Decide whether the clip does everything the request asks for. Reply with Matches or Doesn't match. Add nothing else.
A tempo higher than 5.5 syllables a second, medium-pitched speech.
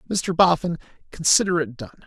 Matches